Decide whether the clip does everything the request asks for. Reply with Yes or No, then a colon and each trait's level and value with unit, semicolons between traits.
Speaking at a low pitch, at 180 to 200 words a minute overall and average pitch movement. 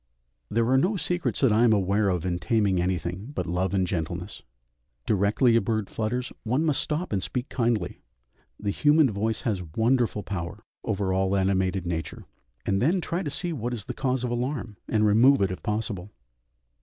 Yes: low, 105 Hz; average, 185 wpm; average, 4.7 semitones